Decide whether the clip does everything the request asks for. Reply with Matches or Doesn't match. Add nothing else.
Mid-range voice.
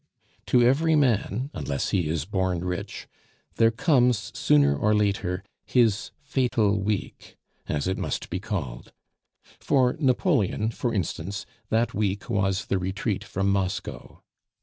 Doesn't match